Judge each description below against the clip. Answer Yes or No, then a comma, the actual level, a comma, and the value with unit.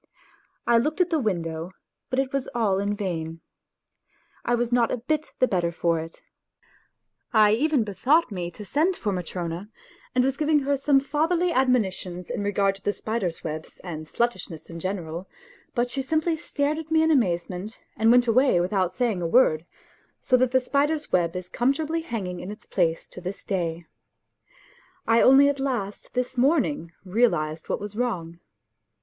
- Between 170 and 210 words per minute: Yes, average, 180 wpm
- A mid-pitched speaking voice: No, high, 220 Hz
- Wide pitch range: Yes, wide, 7.1 semitones